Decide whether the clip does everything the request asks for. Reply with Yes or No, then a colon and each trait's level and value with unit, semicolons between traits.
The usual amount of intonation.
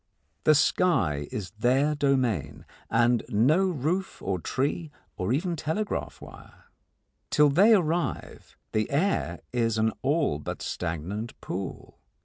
No: wide, 7.2 semitones